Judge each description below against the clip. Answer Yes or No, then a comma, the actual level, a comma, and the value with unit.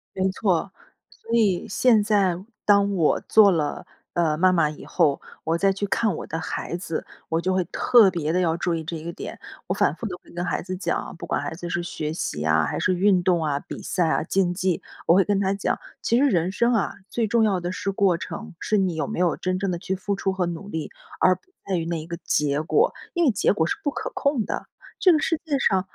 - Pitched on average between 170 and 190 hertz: Yes, medium, 185 Hz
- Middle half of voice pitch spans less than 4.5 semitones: Yes, average, 3.2 semitones